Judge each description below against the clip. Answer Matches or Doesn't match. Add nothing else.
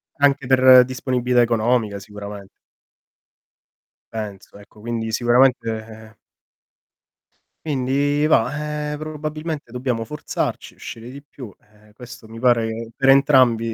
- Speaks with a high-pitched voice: Doesn't match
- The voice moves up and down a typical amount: Matches